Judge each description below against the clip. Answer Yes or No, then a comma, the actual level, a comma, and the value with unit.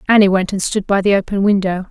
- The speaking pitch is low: No, high, 195 Hz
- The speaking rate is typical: No, fast, 250 wpm